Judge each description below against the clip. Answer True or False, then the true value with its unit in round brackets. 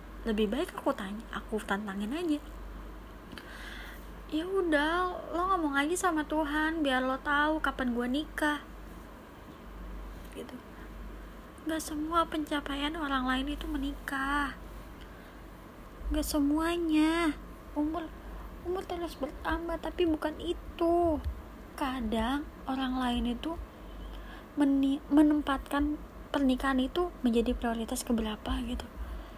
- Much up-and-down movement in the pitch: False (3.4 semitones)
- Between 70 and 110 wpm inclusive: True (100 wpm)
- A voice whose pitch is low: False (290 Hz)